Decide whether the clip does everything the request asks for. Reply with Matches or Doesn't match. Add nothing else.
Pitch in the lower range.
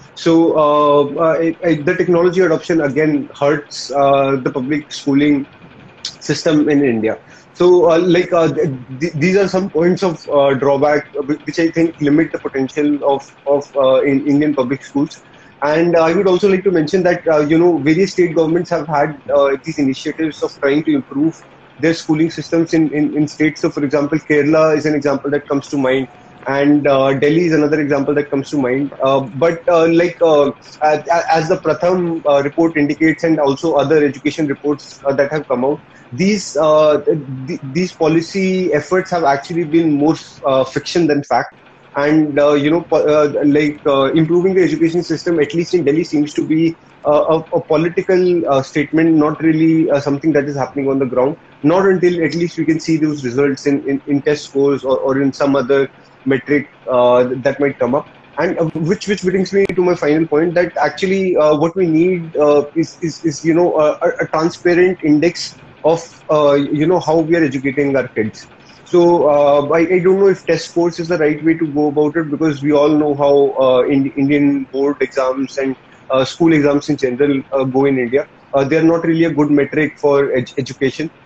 Doesn't match